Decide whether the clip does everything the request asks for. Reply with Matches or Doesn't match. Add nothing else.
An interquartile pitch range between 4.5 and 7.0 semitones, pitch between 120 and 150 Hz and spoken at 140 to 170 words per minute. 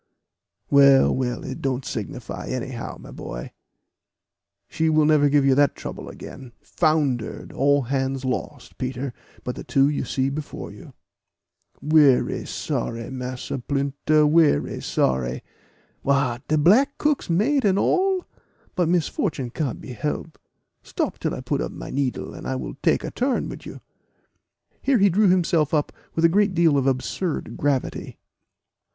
Doesn't match